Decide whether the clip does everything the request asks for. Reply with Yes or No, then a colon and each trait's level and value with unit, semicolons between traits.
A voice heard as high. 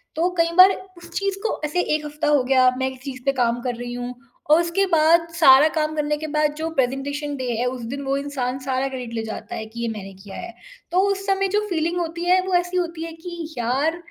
Yes: very high, 295 Hz